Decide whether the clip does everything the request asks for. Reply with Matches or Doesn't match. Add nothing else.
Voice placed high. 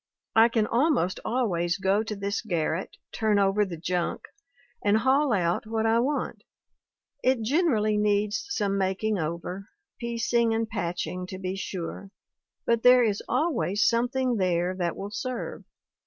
Matches